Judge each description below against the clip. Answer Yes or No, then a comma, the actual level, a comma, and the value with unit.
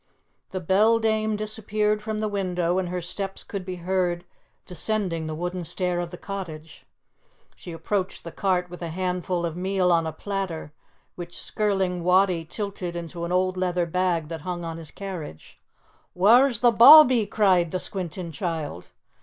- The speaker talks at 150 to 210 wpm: Yes, average, 160 wpm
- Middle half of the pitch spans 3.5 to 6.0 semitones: No, average, 2.7 semitones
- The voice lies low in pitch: No, medium, 180 Hz